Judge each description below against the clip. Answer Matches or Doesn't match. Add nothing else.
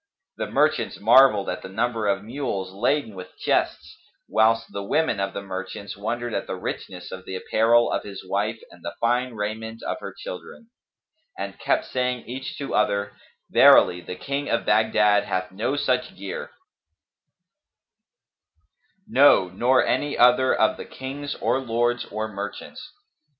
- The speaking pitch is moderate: Doesn't match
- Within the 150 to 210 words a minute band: Matches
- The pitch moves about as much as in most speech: Matches